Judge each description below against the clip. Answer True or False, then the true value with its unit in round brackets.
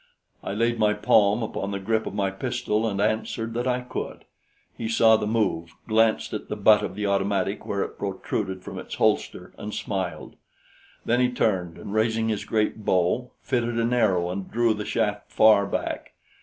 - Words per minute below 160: False (185 wpm)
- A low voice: True (105 Hz)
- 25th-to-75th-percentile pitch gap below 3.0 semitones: True (2.4 semitones)